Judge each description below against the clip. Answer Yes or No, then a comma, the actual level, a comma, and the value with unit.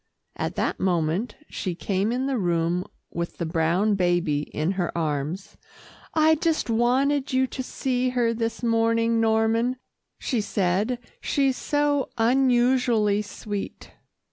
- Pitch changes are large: Yes, wide, 5.8 semitones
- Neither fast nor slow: No, slow, 130 wpm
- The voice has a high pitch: Yes, high, 225 Hz